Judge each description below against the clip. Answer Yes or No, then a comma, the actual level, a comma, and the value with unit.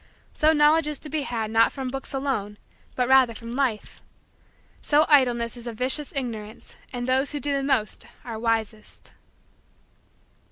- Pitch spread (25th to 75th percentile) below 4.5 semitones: Yes, average, 3.6 semitones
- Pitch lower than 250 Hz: No, very high, 255 Hz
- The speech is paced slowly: No, average, 160 wpm